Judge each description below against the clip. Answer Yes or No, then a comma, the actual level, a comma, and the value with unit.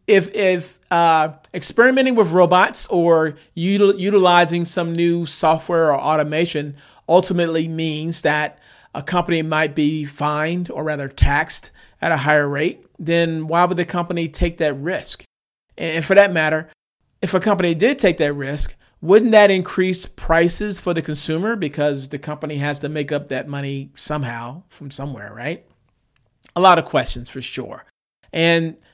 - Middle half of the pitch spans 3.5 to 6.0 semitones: No, average, 3.1 semitones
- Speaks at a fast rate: No, average, 155 wpm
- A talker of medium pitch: Yes, medium, 165 Hz